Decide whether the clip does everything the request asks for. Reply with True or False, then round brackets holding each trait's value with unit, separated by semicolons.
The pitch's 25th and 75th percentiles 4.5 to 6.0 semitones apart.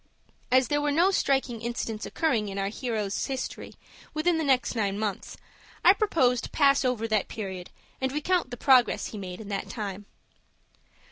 True (5.1 semitones)